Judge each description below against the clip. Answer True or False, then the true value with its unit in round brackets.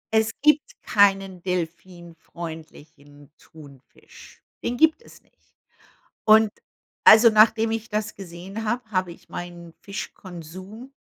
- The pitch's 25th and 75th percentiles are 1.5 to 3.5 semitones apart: False (4.4 semitones)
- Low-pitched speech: False (190 Hz)